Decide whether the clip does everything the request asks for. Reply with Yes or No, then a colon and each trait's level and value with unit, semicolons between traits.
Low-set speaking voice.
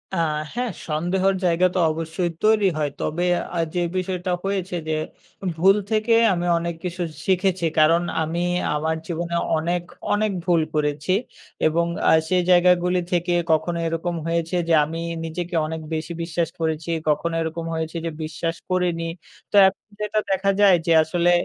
No: medium, 170 Hz